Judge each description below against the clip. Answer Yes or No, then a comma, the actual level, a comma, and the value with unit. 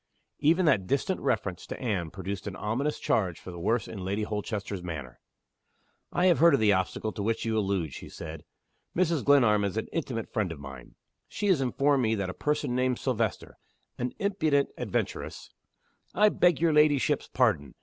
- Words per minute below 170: No, average, 185 wpm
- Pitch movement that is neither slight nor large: No, wide, 6.9 semitones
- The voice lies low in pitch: Yes, low, 110 Hz